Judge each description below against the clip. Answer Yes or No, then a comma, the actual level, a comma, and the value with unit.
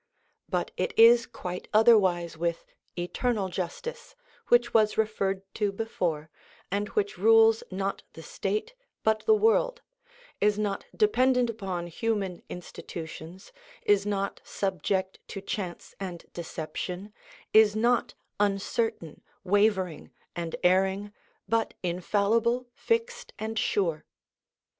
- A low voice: No, high, 205 Hz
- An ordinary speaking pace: No, slow, 110 wpm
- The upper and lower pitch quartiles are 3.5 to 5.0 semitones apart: Yes, average, 3.8 semitones